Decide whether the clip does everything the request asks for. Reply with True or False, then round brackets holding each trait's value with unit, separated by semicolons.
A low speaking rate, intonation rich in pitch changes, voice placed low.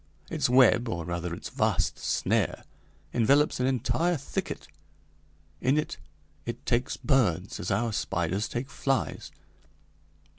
True (120 wpm; 5.9 semitones; 120 Hz)